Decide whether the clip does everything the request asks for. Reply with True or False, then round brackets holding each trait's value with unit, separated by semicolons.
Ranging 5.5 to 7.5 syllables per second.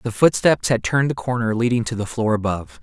True (6.2 syllables/s)